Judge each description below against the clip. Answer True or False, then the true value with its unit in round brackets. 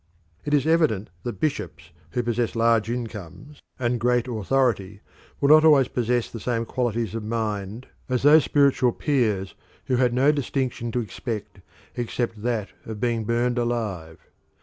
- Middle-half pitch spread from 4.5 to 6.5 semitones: False (2.6 semitones)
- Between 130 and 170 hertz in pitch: False (120 Hz)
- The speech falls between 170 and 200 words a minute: False (150 wpm)